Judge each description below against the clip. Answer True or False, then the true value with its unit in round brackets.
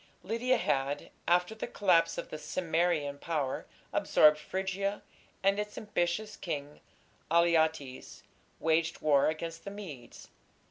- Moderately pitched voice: True (165 Hz)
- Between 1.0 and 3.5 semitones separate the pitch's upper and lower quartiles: False (4.2 semitones)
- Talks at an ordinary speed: False (120 wpm)